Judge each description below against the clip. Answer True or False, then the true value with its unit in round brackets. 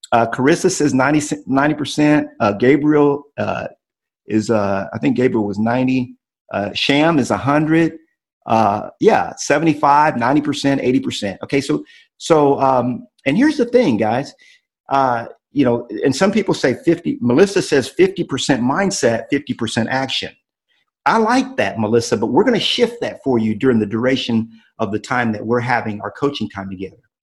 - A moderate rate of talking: True (160 wpm)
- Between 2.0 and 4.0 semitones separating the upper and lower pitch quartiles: False (5.0 semitones)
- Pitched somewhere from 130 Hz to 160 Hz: True (135 Hz)